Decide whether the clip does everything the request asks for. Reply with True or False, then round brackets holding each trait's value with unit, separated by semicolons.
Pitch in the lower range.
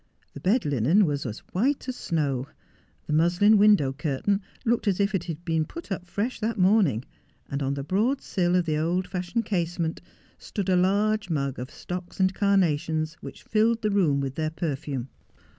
False (180 Hz)